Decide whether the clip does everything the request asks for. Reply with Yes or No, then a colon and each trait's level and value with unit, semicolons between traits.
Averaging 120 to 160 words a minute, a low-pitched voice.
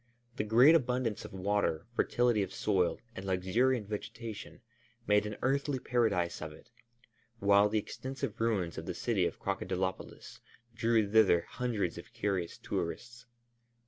Yes: average, 140 wpm; low, 105 Hz